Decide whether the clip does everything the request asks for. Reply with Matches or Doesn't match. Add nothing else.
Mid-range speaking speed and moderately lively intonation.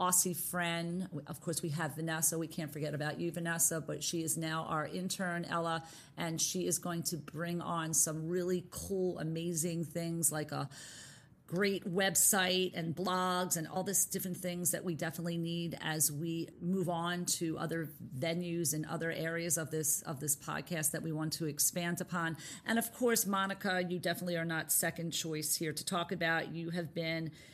Doesn't match